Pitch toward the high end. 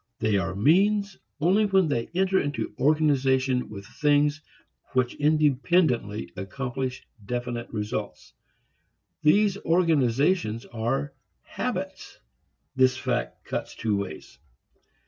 No: low, 135 Hz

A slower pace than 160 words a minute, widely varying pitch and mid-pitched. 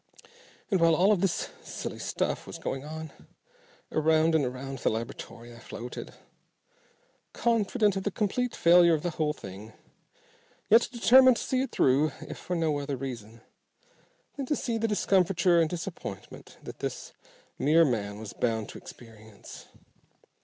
Yes: average, 150 wpm; wide, 7.8 semitones; medium, 160 Hz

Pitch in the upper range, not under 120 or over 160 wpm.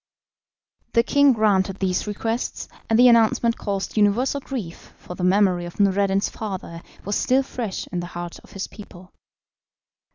Yes: high, 200 Hz; average, 155 wpm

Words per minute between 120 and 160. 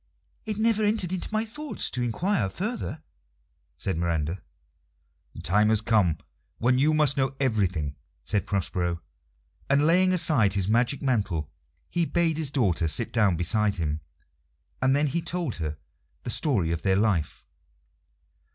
Yes: average, 150 wpm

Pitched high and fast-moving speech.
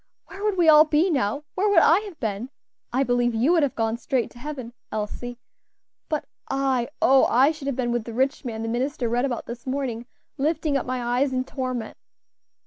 Yes: very high, 260 Hz; fast, 210 wpm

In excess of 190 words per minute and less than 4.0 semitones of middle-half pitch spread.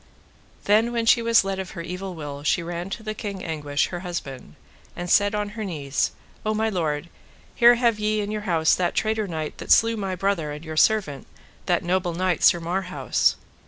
No: average, 200 wpm; average, 4.4 semitones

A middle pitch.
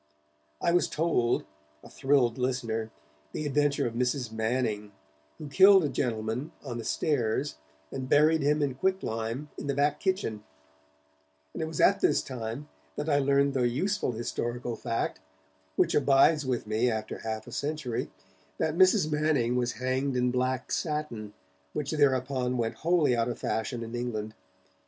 No: low, 130 Hz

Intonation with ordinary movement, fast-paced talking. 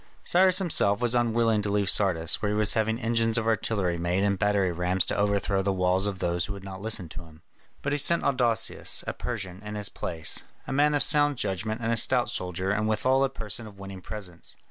Yes: average, 3.5 semitones; fast, 225 wpm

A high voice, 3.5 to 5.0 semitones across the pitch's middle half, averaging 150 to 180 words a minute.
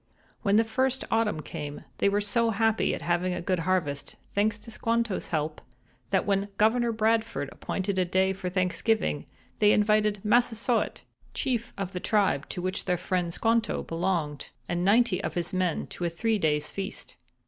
Yes: high, 200 Hz; average, 3.9 semitones; average, 170 wpm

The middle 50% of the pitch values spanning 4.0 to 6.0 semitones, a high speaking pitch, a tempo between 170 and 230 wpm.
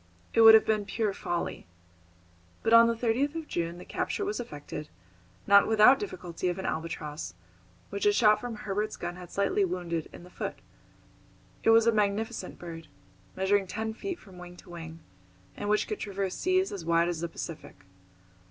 Yes: average, 4.4 semitones; high, 200 Hz; average, 180 wpm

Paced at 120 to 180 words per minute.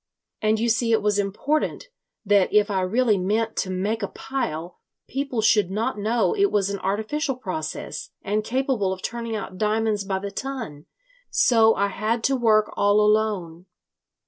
Yes: average, 170 wpm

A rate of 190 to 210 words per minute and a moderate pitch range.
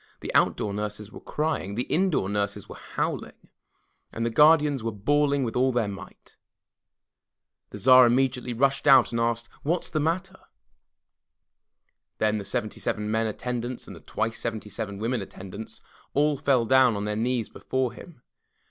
No: average, 165 wpm; average, 4.4 semitones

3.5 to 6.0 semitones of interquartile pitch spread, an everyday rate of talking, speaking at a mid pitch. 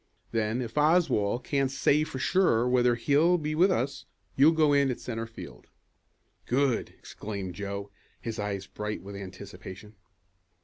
No: wide, 5.5 semitones; average, 145 wpm; low, 120 Hz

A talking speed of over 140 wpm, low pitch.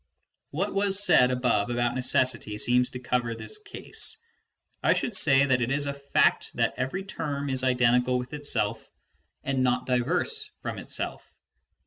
Yes: average, 155 wpm; low, 130 Hz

